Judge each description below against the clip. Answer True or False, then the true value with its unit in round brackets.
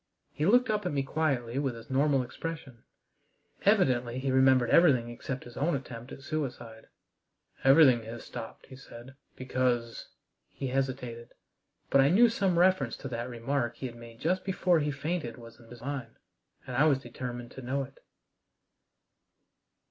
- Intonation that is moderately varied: True (3.6 semitones)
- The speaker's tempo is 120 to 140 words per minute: False (165 wpm)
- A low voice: True (130 Hz)